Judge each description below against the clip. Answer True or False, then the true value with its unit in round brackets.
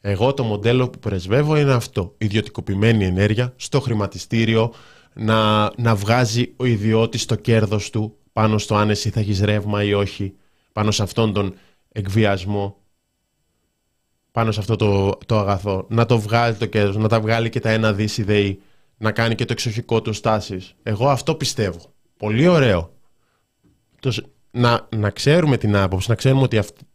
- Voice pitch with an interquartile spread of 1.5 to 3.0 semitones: True (2.5 semitones)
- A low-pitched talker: True (110 Hz)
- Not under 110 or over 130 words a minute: False (155 wpm)